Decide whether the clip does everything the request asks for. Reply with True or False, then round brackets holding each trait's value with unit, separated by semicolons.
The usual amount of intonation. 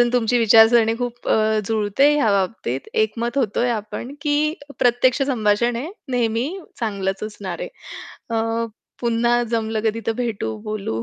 False (2.2 semitones)